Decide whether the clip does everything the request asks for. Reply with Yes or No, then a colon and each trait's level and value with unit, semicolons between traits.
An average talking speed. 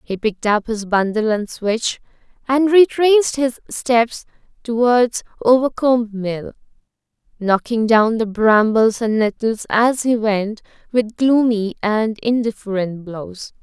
No: slow, 125 wpm